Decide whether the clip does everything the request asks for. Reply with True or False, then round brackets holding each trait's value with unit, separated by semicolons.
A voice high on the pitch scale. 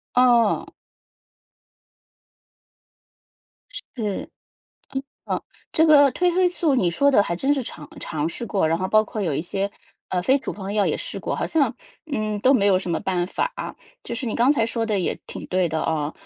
True (210 Hz)